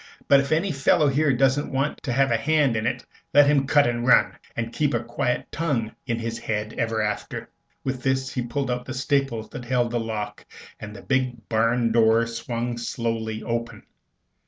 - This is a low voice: Yes, low, 120 Hz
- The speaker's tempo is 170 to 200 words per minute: Yes, average, 195 wpm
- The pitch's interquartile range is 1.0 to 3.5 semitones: Yes, average, 3.0 semitones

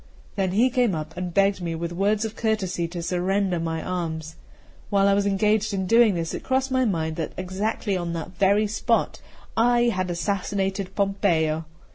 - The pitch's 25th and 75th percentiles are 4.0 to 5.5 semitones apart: No, average, 3.5 semitones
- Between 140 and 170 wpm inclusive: No, average, 180 wpm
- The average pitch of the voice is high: Yes, high, 195 Hz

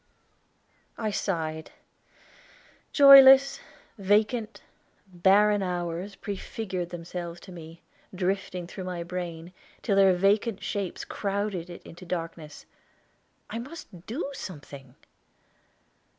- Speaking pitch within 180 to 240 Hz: Yes, medium, 185 Hz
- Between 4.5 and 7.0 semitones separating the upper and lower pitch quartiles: No, average, 3.2 semitones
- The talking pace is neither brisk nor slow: No, slow, 95 wpm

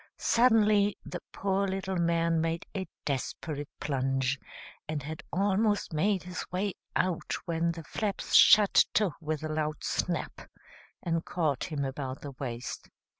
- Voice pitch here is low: No, medium, 165 Hz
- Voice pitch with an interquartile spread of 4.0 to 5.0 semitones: Yes, average, 4.4 semitones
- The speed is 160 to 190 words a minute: No, average, 140 wpm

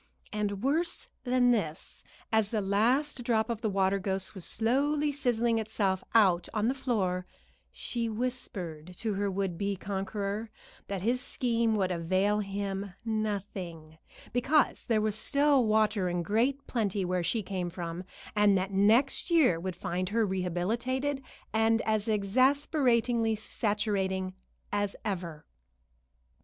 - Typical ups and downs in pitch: Yes, average, 3.7 semitones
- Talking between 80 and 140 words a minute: Yes, slow, 135 wpm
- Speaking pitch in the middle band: No, high, 210 Hz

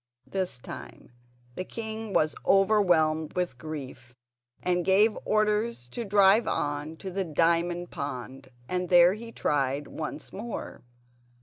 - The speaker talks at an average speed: No, slow, 125 wpm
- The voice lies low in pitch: No, medium, 175 Hz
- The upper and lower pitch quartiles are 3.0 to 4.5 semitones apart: No, average, 5.1 semitones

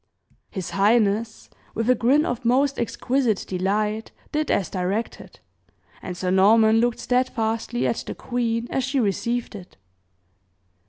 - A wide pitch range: No, average, 3.2 semitones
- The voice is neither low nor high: No, high, 225 Hz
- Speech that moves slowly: Yes, slow, 130 wpm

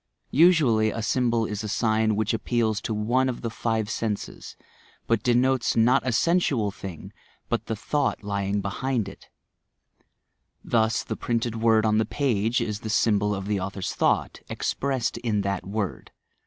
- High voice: No, low, 110 Hz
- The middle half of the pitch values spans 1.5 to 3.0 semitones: Yes, narrow, 2.6 semitones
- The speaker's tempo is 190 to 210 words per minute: No, average, 165 wpm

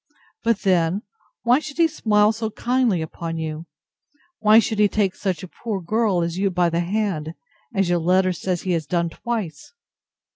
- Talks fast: No, average, 180 wpm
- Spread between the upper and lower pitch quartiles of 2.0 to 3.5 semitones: No, average, 4.3 semitones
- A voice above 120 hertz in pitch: Yes, high, 190 Hz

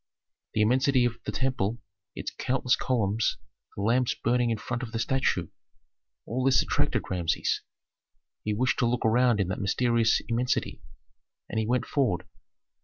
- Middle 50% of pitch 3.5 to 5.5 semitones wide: No, average, 2.9 semitones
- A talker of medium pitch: No, low, 120 Hz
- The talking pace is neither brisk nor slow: Yes, average, 155 wpm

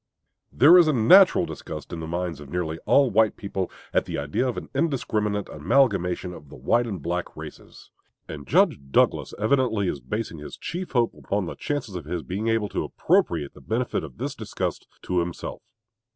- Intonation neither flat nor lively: No, wide, 6.3 semitones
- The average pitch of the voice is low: Yes, low, 100 Hz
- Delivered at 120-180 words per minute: No, average, 190 wpm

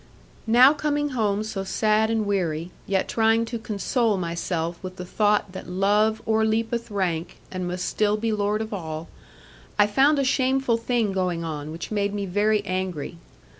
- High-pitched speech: Yes, high, 205 Hz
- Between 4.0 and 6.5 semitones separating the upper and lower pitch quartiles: No, average, 3.4 semitones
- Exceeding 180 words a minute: No, average, 170 wpm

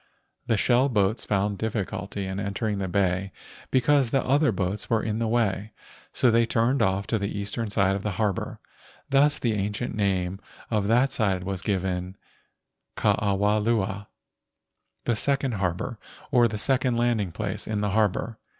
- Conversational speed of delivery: Yes, average, 165 wpm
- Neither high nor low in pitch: No, low, 105 Hz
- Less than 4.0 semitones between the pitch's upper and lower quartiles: Yes, average, 3.1 semitones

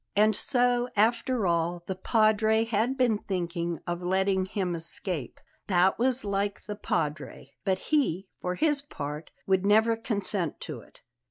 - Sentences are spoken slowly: No, average, 150 wpm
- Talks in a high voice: Yes, high, 200 Hz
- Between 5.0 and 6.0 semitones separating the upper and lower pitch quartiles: No, average, 4.3 semitones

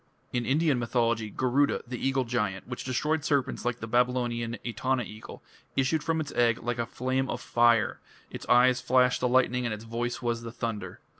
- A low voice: Yes, low, 125 Hz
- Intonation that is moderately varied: No, narrow, 1.7 semitones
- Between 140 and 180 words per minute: No, average, 190 wpm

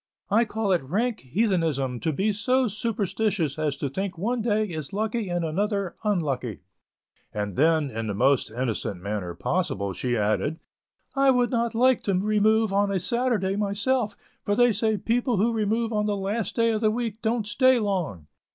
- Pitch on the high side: Yes, high, 205 Hz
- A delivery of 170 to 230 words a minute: Yes, average, 180 wpm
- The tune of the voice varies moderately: No, wide, 6.3 semitones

